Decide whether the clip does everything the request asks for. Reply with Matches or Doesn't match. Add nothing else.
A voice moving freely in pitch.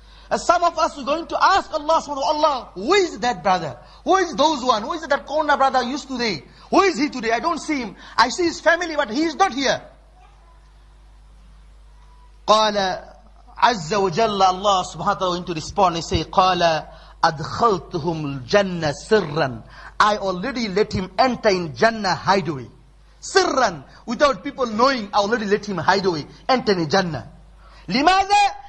Matches